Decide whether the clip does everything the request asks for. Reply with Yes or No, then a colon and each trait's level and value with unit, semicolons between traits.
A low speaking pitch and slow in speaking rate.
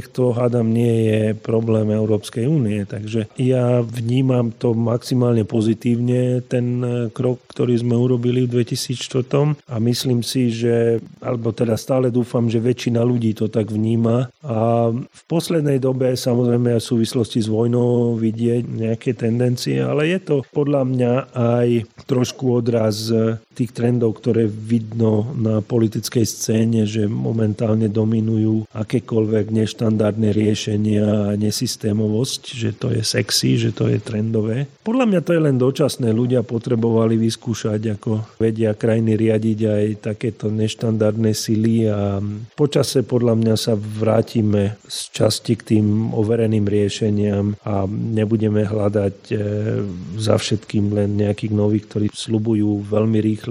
No: low, 115 Hz; average, 130 wpm